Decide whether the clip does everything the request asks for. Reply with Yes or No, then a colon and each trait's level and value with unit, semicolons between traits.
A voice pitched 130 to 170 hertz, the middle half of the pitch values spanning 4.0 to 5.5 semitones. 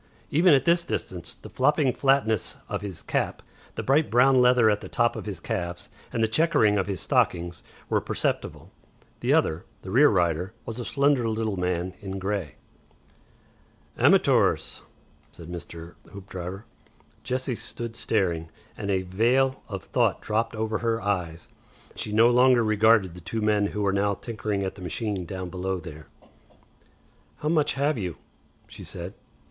No: low, 105 Hz; average, 4.6 semitones